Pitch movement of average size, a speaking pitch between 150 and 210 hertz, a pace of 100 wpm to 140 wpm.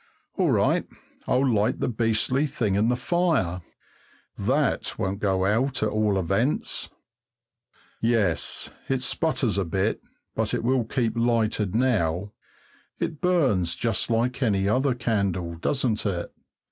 No: average, 4.4 semitones; low, 110 Hz; slow, 135 wpm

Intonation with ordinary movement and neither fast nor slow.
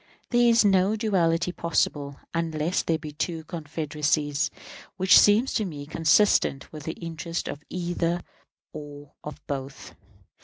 No: average, 3.4 semitones; slow, 130 wpm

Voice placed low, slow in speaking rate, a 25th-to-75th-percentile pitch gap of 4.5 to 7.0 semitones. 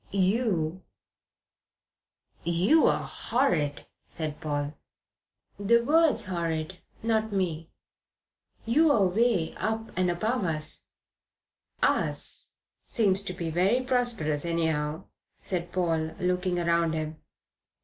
No: medium, 180 Hz; slow, 95 wpm; wide, 5.5 semitones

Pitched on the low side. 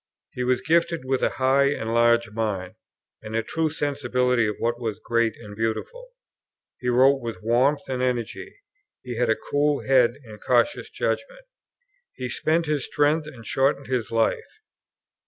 Yes: low, 125 Hz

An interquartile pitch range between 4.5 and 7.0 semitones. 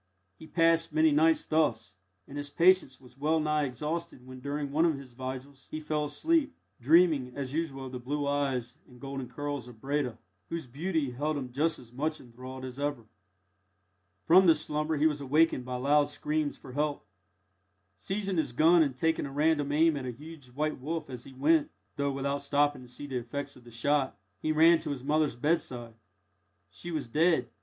No: average, 3.4 semitones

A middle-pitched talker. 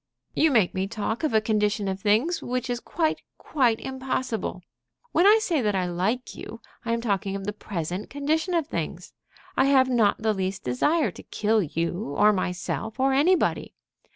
No: high, 220 Hz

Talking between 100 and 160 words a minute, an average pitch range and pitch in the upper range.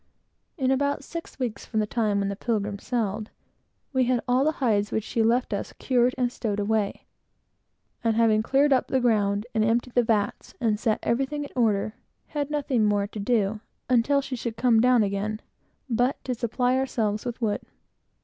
No: average, 190 wpm; average, 3.2 semitones; high, 230 Hz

